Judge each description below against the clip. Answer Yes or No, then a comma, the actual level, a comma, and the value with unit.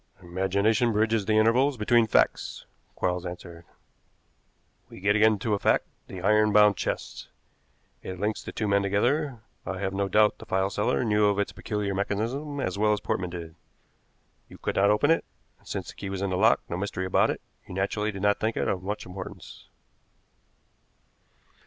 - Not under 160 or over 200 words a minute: Yes, average, 185 wpm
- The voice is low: Yes, low, 100 Hz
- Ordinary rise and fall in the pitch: No, narrow, 2.2 semitones